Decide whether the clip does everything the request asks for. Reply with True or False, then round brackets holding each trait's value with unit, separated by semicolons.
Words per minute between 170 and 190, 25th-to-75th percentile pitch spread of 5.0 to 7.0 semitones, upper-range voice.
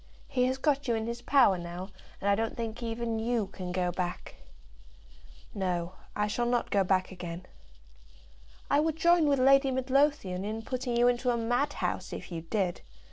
True (180 wpm; 5.5 semitones; 230 Hz)